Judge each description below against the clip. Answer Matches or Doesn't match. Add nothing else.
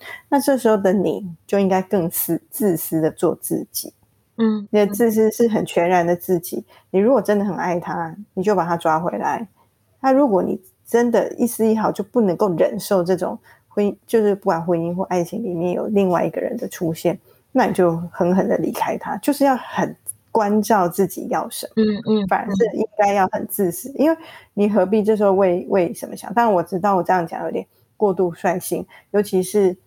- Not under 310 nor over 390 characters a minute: Doesn't match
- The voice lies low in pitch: Doesn't match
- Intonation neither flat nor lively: Matches